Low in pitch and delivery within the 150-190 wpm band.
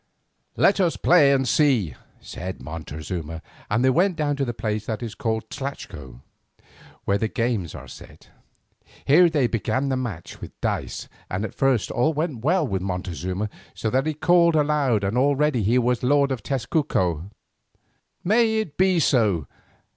Yes: low, 125 Hz; average, 160 wpm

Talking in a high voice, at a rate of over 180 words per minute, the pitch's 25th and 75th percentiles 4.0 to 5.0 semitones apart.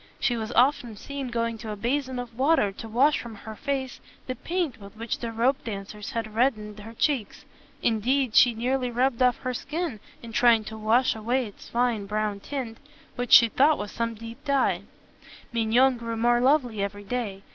No: high, 235 Hz; average, 190 wpm; average, 2.9 semitones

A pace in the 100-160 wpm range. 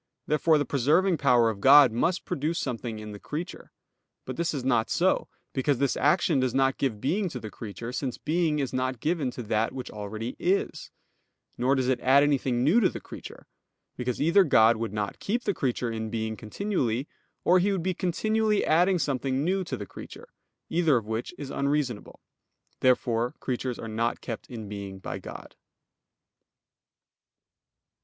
No: average, 175 wpm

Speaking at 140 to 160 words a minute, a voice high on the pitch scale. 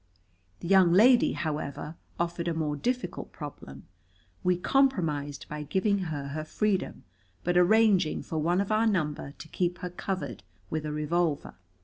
No: average, 150 wpm; medium, 170 Hz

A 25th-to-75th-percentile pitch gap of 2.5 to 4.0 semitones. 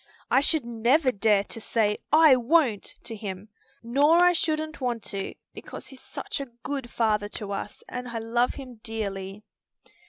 No: average, 4.7 semitones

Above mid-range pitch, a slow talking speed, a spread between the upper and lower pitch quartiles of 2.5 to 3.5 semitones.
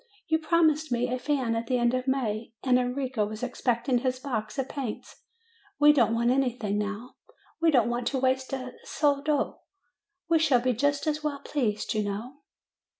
No: very high, 255 Hz; average, 185 wpm; average, 3.1 semitones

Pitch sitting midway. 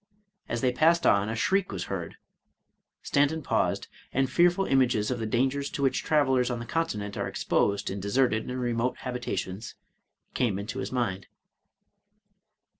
No: low, 125 Hz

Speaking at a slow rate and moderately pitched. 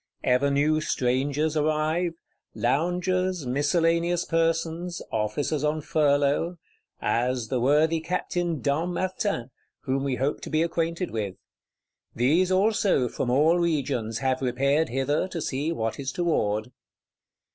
Yes: slow, 115 wpm; medium, 150 Hz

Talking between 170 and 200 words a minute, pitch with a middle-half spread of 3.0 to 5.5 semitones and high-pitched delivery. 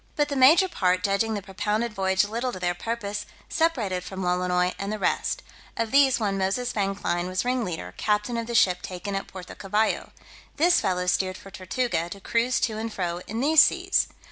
Yes: average, 195 wpm; average, 4.1 semitones; high, 205 Hz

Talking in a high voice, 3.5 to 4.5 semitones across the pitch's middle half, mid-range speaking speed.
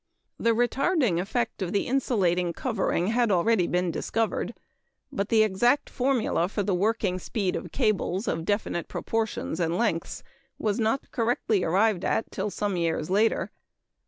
Yes: high, 210 Hz; average, 4.1 semitones; average, 150 wpm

